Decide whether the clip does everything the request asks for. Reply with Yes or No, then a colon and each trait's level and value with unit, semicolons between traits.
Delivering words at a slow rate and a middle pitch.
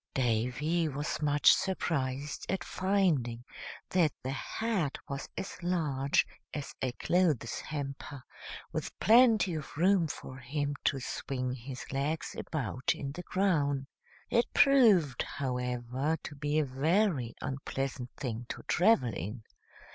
Yes: slow, 125 wpm; medium, 145 Hz